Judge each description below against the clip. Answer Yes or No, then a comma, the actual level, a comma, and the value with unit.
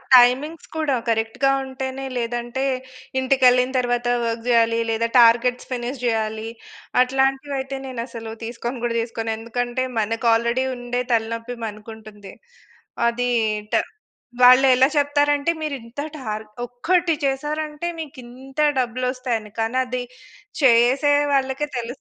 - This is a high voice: Yes, high, 245 Hz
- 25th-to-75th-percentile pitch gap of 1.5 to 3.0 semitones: Yes, narrow, 2.6 semitones